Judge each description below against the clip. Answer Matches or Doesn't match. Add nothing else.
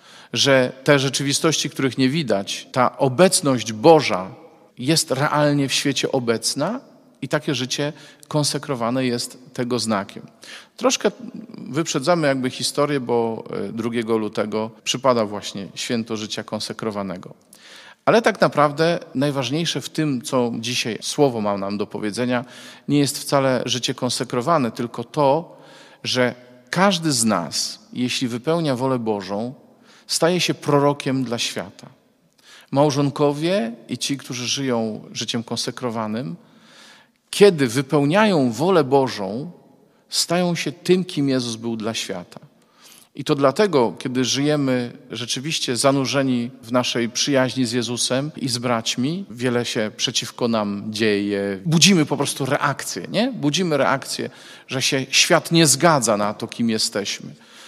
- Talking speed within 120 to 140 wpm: Matches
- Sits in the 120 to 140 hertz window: Matches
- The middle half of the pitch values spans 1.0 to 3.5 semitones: Doesn't match